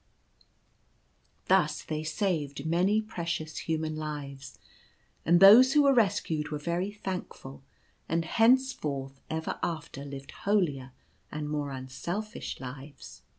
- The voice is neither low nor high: Yes, medium, 160 Hz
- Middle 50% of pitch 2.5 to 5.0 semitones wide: No, wide, 5.5 semitones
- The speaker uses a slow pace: Yes, slow, 110 wpm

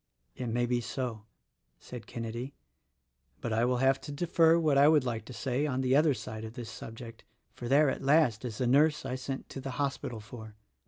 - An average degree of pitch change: Yes, average, 3.3 semitones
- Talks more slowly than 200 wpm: No, fast, 205 wpm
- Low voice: Yes, low, 125 Hz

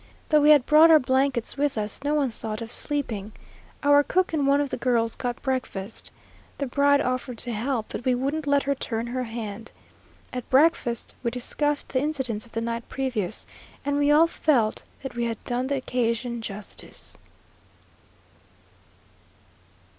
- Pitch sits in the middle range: No, very high, 255 Hz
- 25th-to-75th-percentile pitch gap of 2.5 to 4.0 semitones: Yes, average, 3.6 semitones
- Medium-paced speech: Yes, average, 170 wpm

